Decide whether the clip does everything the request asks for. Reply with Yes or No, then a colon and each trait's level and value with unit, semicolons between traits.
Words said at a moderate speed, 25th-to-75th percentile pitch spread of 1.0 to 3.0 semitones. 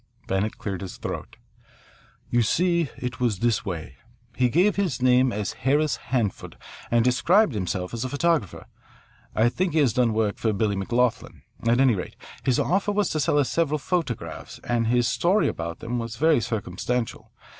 No: average, 175 wpm; wide, 5.6 semitones